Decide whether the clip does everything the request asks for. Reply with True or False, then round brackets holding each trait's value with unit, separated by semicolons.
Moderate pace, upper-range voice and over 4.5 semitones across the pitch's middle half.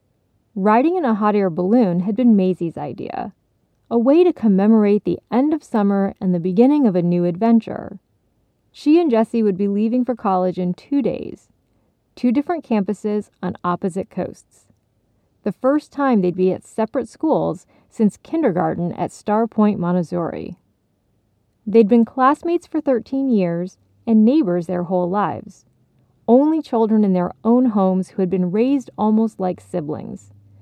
True (155 wpm; 210 Hz; 5.1 semitones)